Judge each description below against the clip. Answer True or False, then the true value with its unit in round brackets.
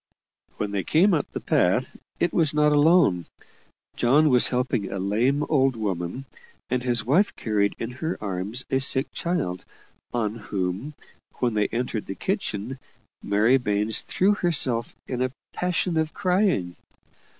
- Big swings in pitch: True (6.6 semitones)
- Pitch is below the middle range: True (125 Hz)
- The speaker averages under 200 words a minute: True (150 wpm)